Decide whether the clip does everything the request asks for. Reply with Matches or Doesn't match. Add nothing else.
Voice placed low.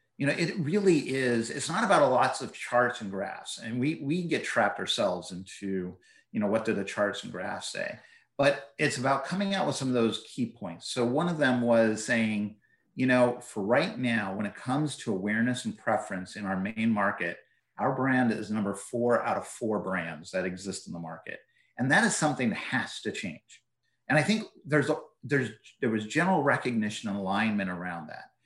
Matches